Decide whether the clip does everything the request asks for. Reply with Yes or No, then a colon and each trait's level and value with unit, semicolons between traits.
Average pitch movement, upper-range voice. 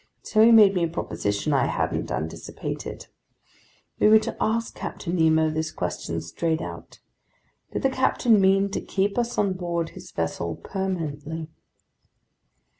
No: average, 4.6 semitones; medium, 175 Hz